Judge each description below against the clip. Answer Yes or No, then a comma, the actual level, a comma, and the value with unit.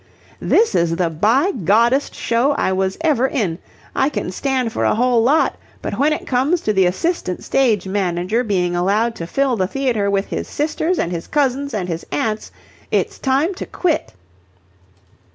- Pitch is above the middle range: Yes, high, 230 Hz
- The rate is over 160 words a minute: Yes, average, 175 wpm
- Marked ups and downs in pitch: Yes, wide, 6.6 semitones